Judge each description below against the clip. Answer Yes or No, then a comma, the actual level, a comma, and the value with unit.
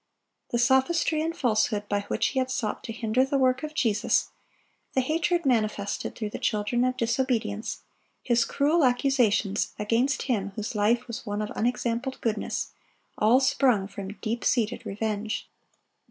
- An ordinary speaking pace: Yes, average, 155 wpm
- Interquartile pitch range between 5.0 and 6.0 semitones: No, average, 3.6 semitones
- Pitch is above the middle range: Yes, high, 235 Hz